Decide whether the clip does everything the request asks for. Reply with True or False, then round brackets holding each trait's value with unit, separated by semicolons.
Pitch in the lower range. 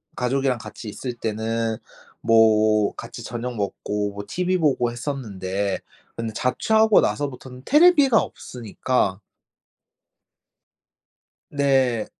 True (120 Hz)